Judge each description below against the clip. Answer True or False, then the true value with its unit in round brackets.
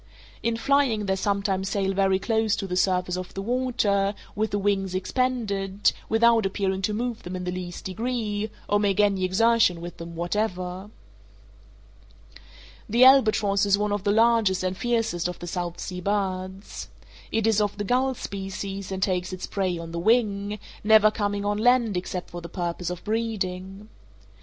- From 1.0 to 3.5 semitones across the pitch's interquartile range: True (2.9 semitones)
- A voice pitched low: False (200 Hz)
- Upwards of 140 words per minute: True (170 wpm)